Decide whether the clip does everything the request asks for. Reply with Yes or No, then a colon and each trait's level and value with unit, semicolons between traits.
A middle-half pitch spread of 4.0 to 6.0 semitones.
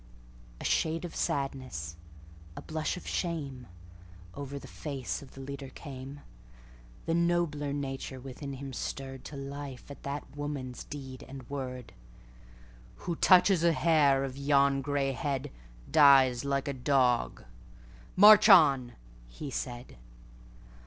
No: average, 2.7 semitones